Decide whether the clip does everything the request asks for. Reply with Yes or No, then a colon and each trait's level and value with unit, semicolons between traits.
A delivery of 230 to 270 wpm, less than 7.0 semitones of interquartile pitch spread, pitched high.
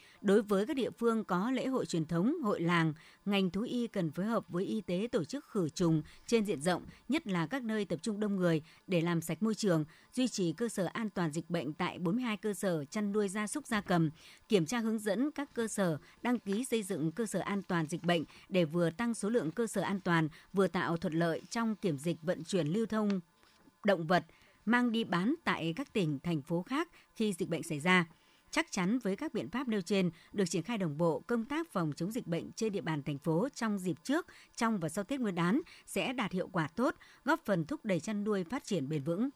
Yes: average, 245 wpm; average, 5.1 semitones; high, 195 Hz